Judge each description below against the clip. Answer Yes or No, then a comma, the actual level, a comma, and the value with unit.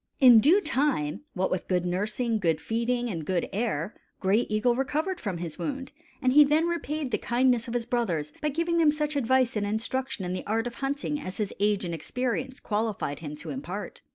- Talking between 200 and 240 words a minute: Yes, fast, 205 wpm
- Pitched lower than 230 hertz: No, high, 235 Hz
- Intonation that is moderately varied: No, wide, 6.1 semitones